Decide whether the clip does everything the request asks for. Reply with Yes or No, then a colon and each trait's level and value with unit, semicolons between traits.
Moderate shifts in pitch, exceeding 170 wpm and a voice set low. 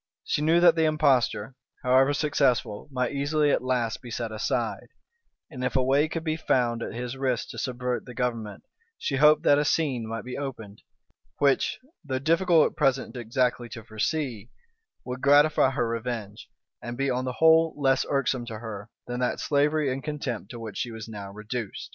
Yes: average, 3.6 semitones; average, 185 wpm; low, 130 Hz